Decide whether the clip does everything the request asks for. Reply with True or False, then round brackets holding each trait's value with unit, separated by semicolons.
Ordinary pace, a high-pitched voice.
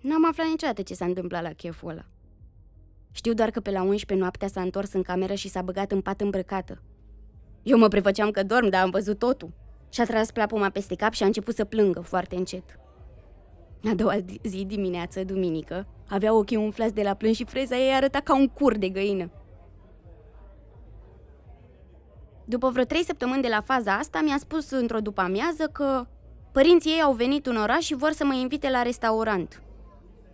False (185 wpm; 205 Hz)